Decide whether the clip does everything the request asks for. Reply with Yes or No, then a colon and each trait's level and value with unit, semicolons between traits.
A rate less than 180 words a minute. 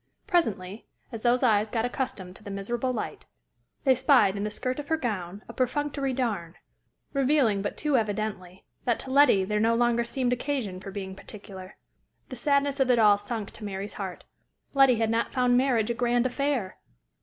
No: average, 185 wpm